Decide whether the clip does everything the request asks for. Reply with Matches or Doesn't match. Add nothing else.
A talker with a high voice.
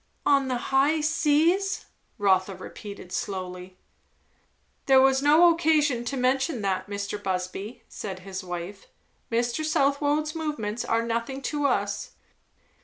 Matches